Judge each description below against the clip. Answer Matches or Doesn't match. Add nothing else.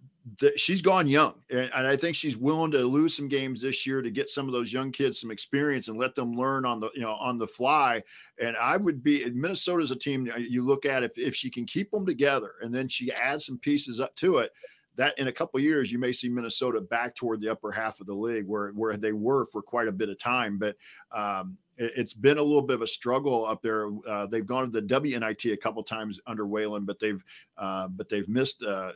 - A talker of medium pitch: Doesn't match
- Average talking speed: Doesn't match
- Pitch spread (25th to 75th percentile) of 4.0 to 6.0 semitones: Matches